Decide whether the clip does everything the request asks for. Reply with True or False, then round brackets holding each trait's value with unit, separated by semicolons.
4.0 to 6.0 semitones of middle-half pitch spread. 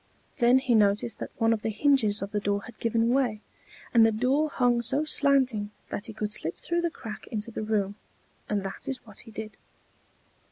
False (3.4 semitones)